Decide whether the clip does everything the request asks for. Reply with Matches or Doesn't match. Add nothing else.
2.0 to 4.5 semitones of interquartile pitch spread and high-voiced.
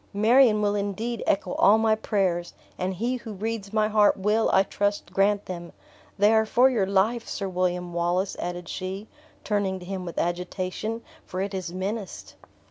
Matches